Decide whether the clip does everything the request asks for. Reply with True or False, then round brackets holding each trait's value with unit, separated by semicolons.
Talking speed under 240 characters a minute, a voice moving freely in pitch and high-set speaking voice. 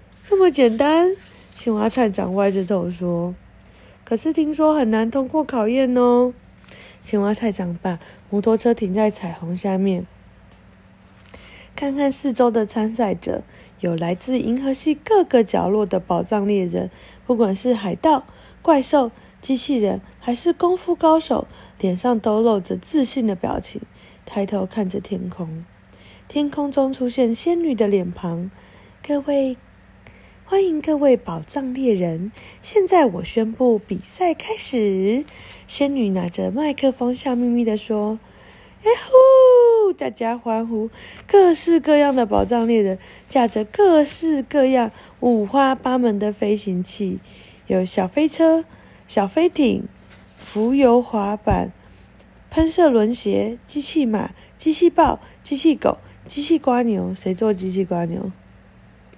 True (200 characters per minute; 6.4 semitones; 235 Hz)